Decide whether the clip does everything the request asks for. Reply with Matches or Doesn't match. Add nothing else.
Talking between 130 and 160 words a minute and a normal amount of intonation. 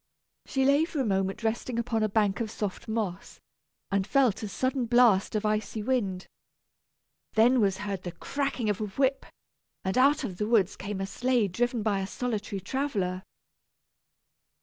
Doesn't match